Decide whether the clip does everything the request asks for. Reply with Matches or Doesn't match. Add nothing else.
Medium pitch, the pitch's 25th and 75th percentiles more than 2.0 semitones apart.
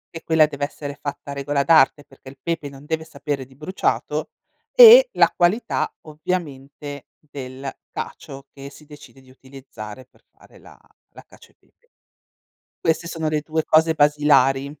Matches